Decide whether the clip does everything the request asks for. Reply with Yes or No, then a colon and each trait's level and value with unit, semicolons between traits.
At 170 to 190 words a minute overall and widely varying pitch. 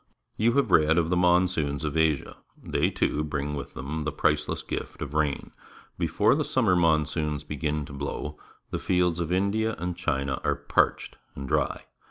No: average, 175 wpm; average, 3.5 semitones